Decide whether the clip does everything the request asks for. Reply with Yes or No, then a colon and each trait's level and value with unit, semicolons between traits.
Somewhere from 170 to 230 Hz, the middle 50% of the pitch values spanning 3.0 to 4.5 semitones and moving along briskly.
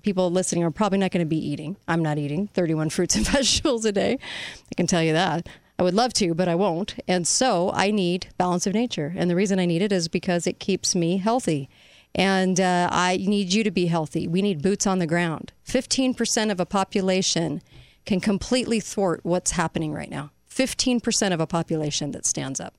Yes: medium, 185 Hz; average, 3.3 semitones; fast, 215 wpm